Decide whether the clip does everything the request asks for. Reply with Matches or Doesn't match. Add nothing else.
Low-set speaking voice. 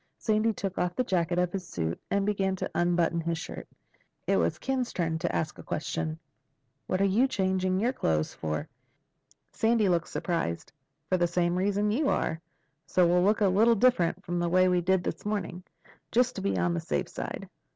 Doesn't match